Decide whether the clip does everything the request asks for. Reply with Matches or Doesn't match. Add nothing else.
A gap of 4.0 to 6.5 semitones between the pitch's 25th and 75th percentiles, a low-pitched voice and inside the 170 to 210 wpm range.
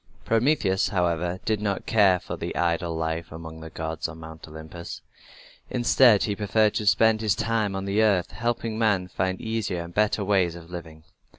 Matches